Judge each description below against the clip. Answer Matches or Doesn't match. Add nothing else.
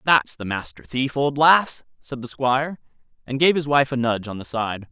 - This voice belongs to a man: Matches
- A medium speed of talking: Doesn't match